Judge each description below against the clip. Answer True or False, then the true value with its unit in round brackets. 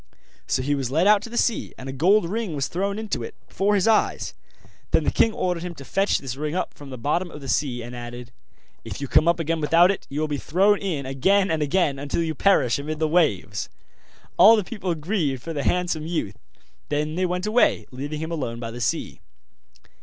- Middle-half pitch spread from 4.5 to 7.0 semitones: True (5.3 semitones)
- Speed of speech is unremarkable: False (230 wpm)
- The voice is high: False (160 Hz)